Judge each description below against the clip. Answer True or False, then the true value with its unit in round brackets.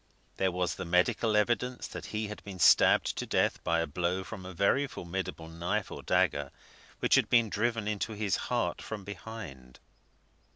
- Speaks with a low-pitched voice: True (100 Hz)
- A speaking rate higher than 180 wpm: False (175 wpm)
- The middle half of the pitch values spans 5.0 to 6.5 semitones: False (3.9 semitones)